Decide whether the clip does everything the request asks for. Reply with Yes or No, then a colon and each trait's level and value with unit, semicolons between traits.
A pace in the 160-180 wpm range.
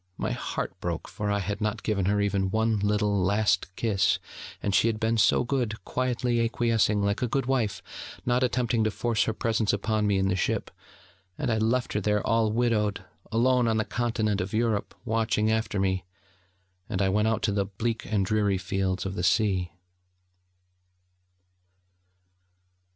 Yes: average, 175 wpm